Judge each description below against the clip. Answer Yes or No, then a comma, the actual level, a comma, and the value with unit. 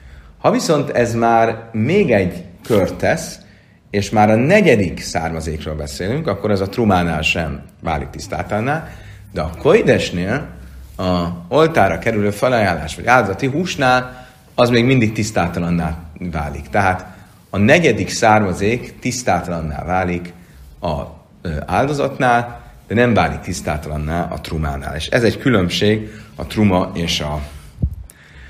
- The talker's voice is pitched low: Yes, very low, 95 Hz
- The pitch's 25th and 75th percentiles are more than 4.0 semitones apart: Yes, wide, 5.5 semitones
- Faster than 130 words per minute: No, average, 120 wpm